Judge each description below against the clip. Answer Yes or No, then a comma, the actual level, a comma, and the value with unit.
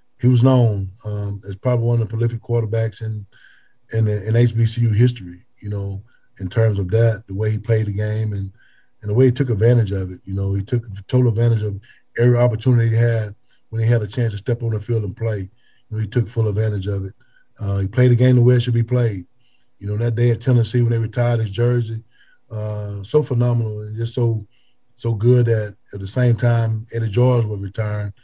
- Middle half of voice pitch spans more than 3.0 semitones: No, narrow, 2.5 semitones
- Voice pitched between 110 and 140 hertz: Yes, low, 115 Hz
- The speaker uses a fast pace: Yes, fast, 230 wpm